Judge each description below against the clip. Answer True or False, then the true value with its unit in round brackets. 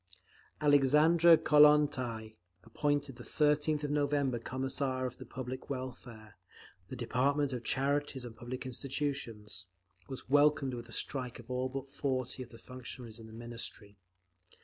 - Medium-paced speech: False (125 wpm)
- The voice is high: False (130 Hz)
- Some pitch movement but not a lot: True (3.4 semitones)